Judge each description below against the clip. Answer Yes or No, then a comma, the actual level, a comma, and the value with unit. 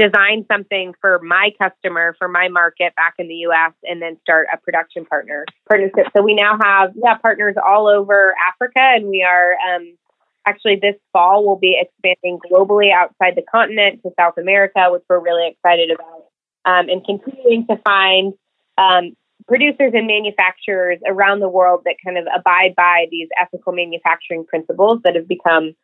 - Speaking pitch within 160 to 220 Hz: Yes, medium, 185 Hz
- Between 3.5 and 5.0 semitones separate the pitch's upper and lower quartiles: No, average, 2.7 semitones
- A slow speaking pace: No, average, 175 wpm